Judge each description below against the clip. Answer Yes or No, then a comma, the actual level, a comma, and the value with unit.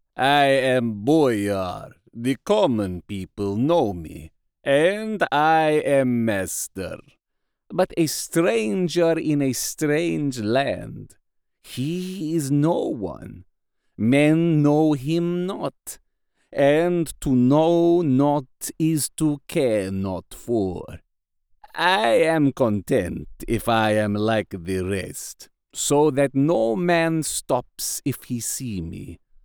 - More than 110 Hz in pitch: Yes, medium, 140 Hz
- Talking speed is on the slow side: Yes, slow, 110 wpm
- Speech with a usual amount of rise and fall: No, wide, 6.2 semitones